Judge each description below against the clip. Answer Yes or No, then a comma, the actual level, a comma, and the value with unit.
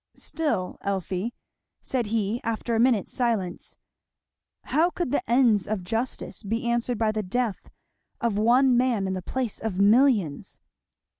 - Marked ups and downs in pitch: No, average, 3.6 semitones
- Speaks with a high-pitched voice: Yes, high, 225 Hz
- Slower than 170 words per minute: Yes, average, 145 wpm